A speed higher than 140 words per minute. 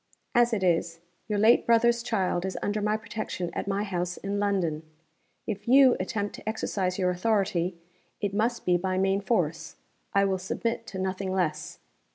Yes: average, 175 wpm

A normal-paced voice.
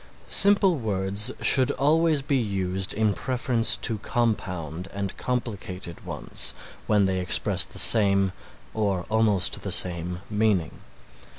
No: slow, 120 wpm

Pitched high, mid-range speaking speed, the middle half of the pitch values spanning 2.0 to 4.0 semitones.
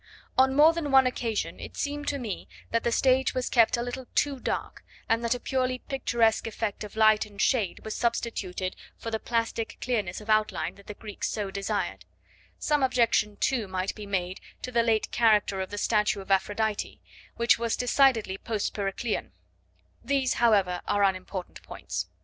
Yes: high, 225 Hz; average, 180 wpm; average, 3.6 semitones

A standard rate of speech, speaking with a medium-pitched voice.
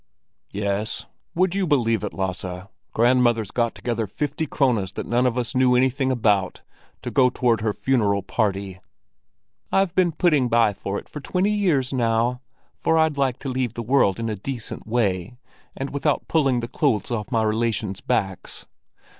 No: average, 165 wpm; low, 120 Hz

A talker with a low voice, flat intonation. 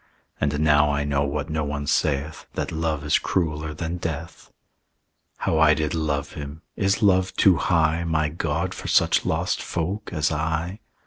Yes: very low, 80 Hz; narrow, 2.2 semitones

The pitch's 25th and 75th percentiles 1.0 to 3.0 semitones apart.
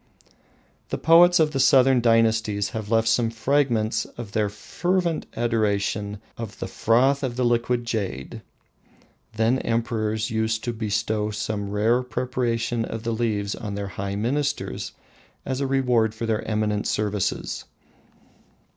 Yes: narrow, 2.6 semitones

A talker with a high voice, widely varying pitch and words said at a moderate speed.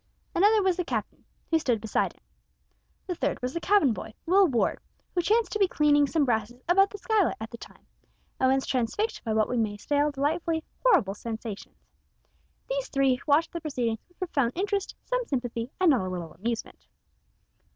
Yes: very high, 285 Hz; wide, 7.8 semitones; average, 185 wpm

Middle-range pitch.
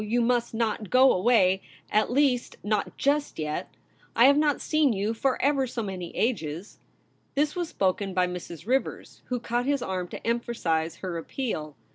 No: high, 230 Hz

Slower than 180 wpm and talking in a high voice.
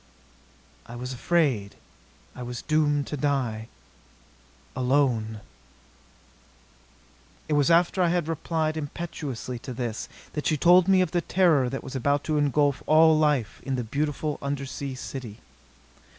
No: slow, 135 wpm; medium, 145 Hz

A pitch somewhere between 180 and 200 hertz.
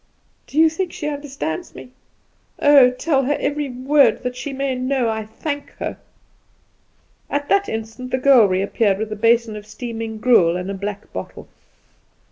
No: very high, 250 Hz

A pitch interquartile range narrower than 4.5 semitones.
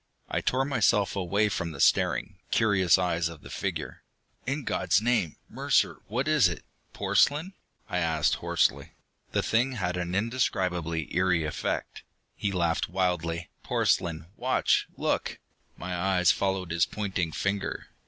Yes: average, 4.0 semitones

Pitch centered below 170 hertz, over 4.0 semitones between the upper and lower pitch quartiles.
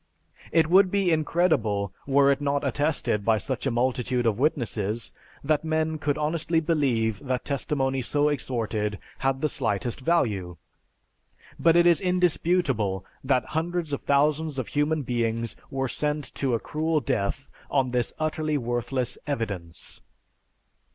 Yes: medium, 140 Hz; average, 4.8 semitones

